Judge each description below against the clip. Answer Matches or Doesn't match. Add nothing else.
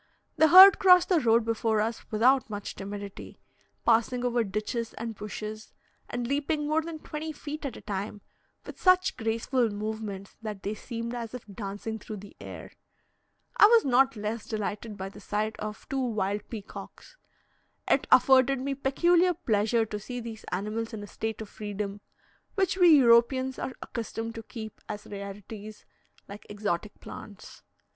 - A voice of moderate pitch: Doesn't match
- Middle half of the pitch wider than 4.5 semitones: Doesn't match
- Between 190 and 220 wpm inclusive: Doesn't match